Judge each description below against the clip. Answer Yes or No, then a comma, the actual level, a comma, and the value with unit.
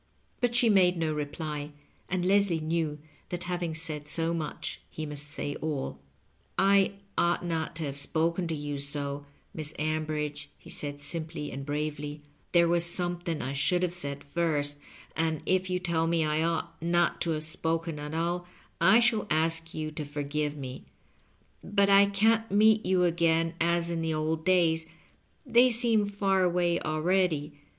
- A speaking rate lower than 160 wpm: No, average, 175 wpm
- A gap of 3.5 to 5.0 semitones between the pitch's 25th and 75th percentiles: No, average, 2.9 semitones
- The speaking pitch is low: No, medium, 165 Hz